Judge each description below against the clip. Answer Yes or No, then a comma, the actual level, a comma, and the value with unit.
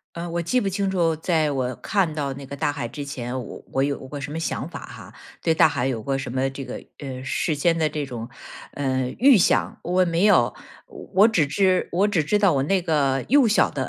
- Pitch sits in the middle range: Yes, medium, 150 Hz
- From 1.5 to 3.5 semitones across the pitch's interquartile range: No, average, 5.1 semitones